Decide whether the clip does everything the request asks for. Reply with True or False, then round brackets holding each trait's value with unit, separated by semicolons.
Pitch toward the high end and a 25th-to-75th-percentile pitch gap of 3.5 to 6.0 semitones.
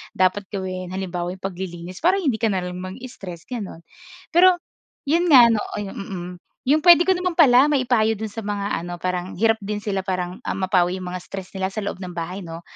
True (195 Hz; 4.3 semitones)